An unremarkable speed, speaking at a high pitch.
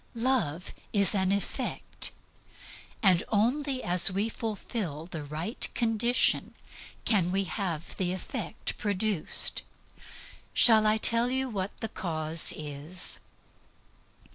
No: slow, 110 wpm; high, 195 Hz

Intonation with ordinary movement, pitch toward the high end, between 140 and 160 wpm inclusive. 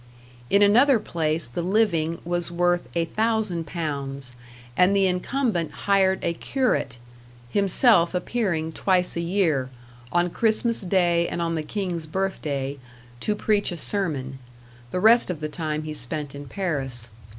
No: average, 4.4 semitones; medium, 175 Hz; average, 150 wpm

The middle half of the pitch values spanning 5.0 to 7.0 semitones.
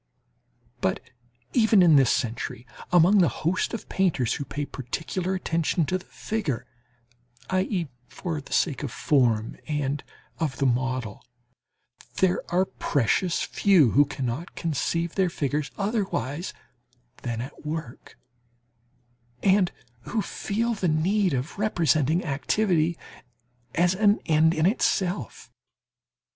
Yes: average, 5.3 semitones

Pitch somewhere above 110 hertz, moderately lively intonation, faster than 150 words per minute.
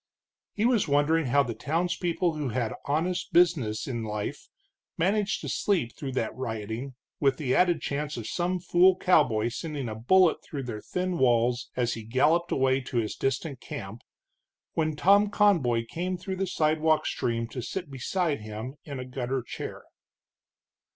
No: medium, 140 Hz; wide, 6.3 semitones; average, 165 wpm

